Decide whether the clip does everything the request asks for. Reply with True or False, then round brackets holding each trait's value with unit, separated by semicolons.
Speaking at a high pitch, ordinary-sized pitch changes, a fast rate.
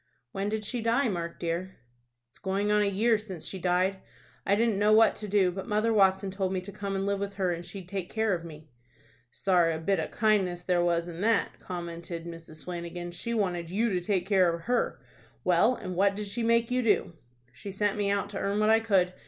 True (195 Hz; 3.1 semitones; 230 wpm)